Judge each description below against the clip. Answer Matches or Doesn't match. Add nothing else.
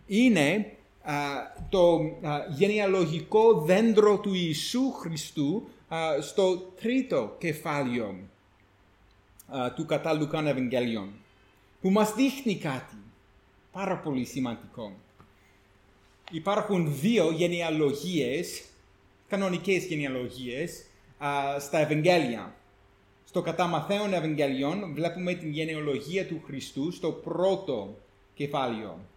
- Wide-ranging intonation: Matches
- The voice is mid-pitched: Matches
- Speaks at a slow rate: Matches